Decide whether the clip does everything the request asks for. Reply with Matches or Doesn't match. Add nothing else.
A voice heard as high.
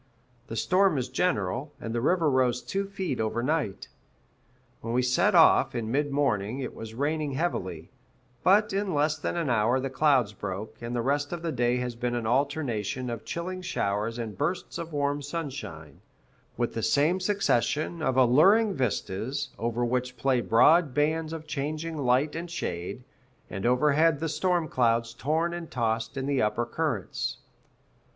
Doesn't match